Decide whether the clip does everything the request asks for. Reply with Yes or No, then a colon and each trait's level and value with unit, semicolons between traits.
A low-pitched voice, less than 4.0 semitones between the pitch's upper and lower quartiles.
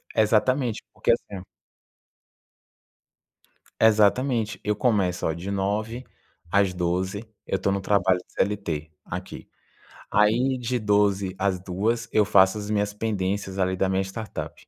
Yes: low, 100 Hz; narrow, 2.5 semitones